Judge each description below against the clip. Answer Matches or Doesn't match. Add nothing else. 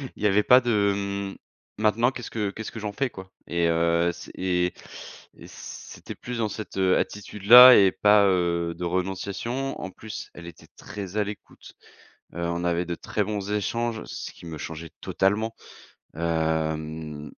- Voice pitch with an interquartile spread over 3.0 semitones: Matches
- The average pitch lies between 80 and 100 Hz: Matches